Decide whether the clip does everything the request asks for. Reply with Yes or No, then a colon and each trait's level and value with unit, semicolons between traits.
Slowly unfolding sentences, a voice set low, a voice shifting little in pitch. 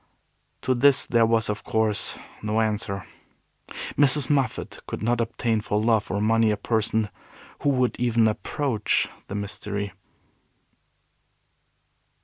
Yes: slow, 125 wpm; low, 110 Hz; narrow, 2.3 semitones